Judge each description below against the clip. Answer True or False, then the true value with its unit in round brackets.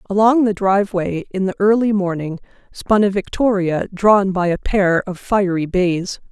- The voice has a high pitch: True (195 Hz)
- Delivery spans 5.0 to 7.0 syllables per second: False (4.5 syllables/s)